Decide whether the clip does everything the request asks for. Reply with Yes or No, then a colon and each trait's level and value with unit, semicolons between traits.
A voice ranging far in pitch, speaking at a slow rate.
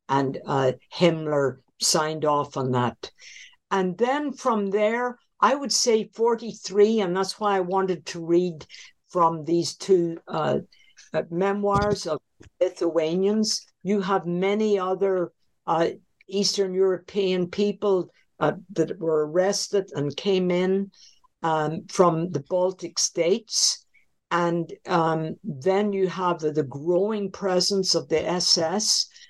No: average, 3.3 semitones; slow, 125 wpm